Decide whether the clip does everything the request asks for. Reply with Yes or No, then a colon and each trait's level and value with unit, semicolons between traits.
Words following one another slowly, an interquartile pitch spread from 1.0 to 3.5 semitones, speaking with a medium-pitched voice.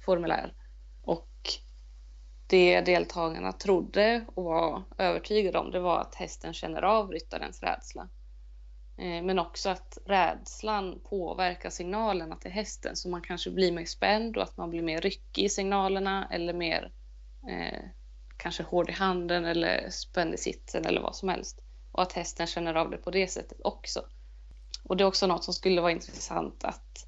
No: average, 165 wpm; average, 3.0 semitones; medium, 175 Hz